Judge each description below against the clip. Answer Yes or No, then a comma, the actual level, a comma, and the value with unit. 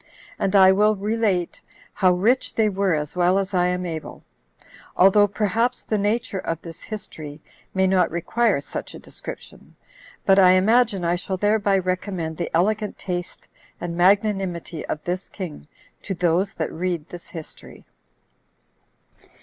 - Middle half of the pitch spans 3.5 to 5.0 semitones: No, average, 2.8 semitones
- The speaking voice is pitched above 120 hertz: Yes, medium, 185 Hz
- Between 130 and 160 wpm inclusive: Yes, average, 150 wpm